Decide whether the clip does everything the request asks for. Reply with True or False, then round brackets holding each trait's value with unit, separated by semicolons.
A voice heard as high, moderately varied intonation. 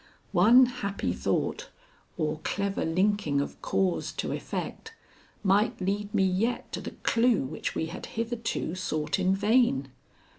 True (195 Hz; 4.5 semitones)